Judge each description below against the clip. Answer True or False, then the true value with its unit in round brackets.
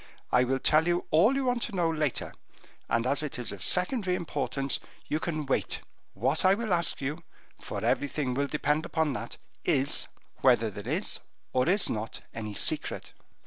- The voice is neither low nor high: True (150 Hz)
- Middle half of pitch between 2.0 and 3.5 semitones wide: False (5.2 semitones)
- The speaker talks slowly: False (175 wpm)